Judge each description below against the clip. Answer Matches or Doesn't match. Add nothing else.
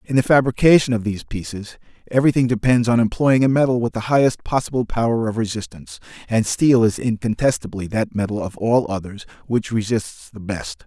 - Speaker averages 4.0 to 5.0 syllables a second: Doesn't match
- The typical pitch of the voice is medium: Doesn't match